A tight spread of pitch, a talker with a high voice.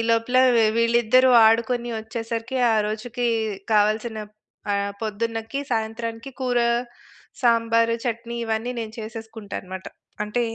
Yes: narrow, 1.4 semitones; high, 230 Hz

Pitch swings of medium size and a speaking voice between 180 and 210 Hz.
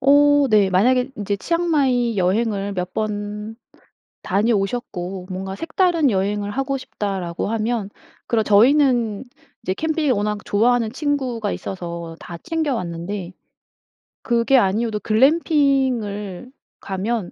No: average, 5.0 semitones; high, 220 Hz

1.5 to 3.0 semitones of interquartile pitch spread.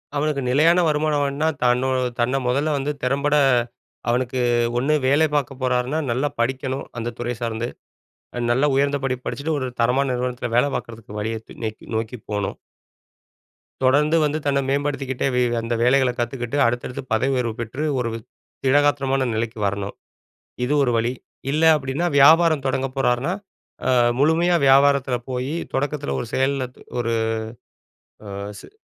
Yes: average, 2.7 semitones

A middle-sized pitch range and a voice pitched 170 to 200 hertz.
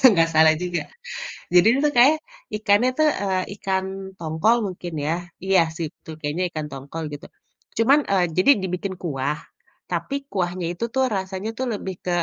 Yes: average, 3.7 semitones; medium, 185 Hz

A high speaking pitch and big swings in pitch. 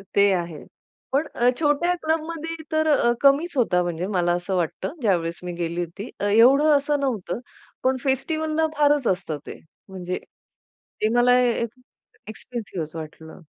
Yes: high, 235 Hz; wide, 8.6 semitones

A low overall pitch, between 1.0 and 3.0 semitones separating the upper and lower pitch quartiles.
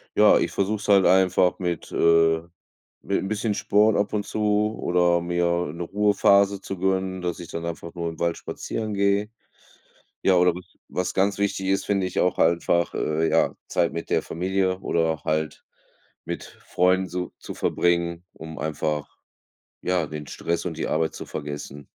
Yes: very low, 90 Hz; average, 2.7 semitones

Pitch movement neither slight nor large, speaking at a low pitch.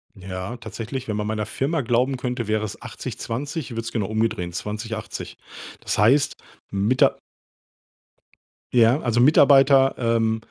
Yes: average, 3.3 semitones; low, 115 Hz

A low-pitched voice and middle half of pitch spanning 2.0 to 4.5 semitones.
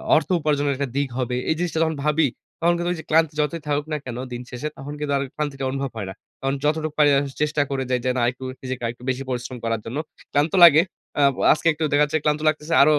No: medium, 145 Hz; average, 2.9 semitones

